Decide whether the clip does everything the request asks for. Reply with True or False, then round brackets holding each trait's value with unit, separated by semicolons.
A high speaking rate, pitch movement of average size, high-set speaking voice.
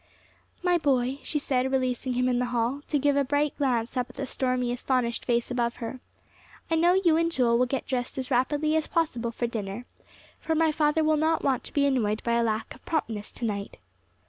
True (220 wpm; 3.8 semitones; 255 Hz)